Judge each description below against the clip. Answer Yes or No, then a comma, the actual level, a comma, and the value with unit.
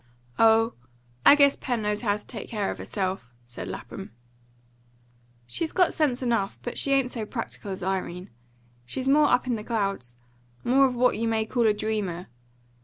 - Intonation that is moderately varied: Yes, average, 4.3 semitones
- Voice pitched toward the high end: Yes, high, 225 Hz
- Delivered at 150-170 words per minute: No, average, 180 wpm